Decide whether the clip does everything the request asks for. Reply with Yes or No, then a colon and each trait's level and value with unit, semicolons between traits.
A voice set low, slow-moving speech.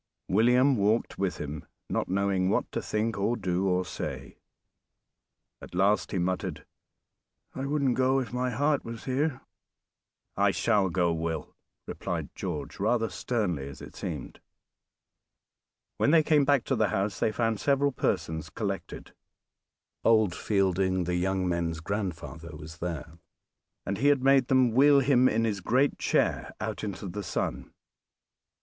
No: low, 105 Hz; average, 145 wpm